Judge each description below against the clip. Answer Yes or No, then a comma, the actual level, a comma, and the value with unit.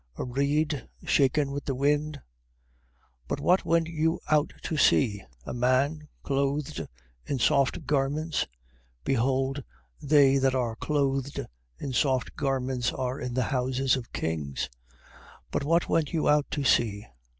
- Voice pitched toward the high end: No, low, 135 Hz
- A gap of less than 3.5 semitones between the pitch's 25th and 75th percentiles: Yes, narrow, 2.6 semitones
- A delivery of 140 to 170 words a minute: Yes, average, 145 wpm